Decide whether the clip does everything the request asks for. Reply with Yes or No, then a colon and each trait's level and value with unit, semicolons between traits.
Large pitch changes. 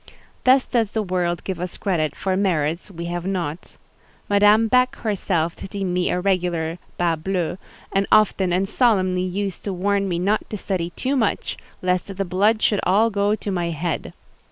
No: average, 2.7 semitones